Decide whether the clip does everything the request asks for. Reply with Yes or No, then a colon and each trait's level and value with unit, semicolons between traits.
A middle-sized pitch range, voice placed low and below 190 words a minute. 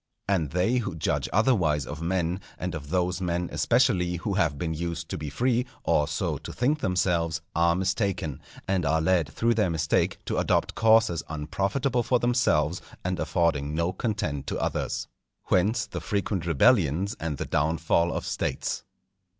Yes: average, 4.0 semitones; very low, 90 Hz; average, 165 wpm